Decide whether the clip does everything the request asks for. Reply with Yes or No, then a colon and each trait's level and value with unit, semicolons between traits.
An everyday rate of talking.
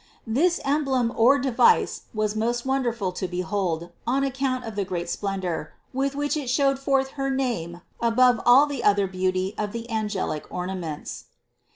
Yes: average, 170 wpm